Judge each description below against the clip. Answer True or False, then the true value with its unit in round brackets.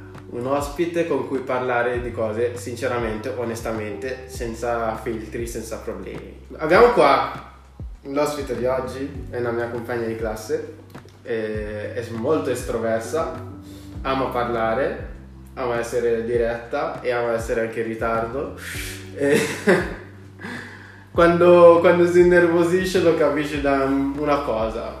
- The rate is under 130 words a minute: True (115 wpm)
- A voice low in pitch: True (120 Hz)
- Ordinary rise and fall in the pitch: True (3.9 semitones)